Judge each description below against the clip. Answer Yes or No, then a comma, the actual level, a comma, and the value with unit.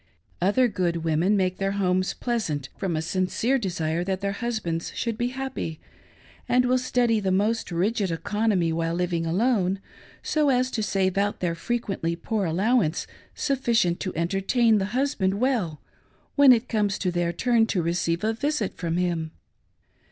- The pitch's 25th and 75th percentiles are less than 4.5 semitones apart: No, average, 5.3 semitones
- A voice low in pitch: No, high, 195 Hz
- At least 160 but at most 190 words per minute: Yes, average, 165 wpm